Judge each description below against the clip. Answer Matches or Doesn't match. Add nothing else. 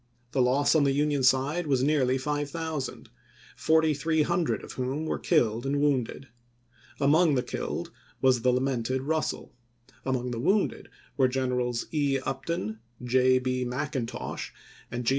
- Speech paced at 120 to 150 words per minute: Matches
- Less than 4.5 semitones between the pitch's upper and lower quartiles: Matches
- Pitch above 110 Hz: Matches